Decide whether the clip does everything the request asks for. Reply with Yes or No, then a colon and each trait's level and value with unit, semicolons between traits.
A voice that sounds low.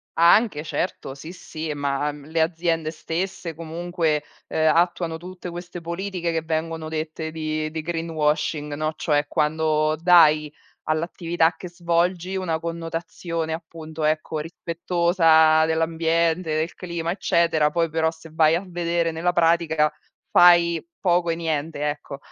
No: medium, 165 Hz